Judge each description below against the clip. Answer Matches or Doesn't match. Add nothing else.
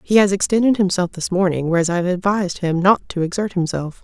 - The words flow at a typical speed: Doesn't match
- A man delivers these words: Doesn't match